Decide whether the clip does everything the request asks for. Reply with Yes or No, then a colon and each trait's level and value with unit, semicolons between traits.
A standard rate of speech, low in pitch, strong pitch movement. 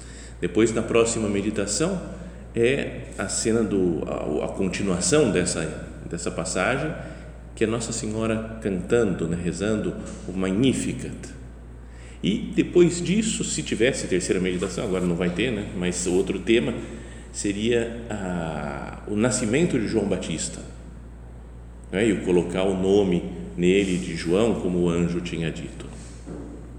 Yes: average, 130 wpm; very low, 90 Hz; wide, 6.0 semitones